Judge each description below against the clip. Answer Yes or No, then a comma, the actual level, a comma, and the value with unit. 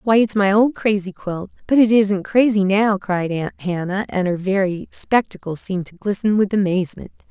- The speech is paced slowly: No, average, 190 wpm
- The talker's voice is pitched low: No, high, 200 Hz